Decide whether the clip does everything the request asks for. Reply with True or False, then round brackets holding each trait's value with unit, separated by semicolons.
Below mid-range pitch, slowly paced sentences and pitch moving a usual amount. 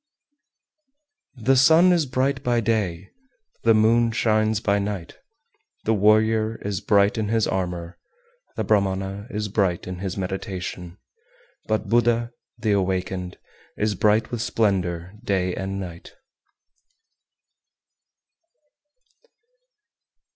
True (105 Hz; 110 wpm; 3.1 semitones)